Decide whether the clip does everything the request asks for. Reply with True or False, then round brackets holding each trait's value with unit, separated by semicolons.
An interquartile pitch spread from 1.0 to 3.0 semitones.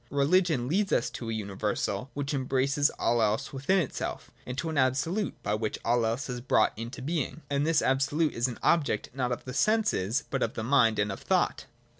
False (4.3 semitones)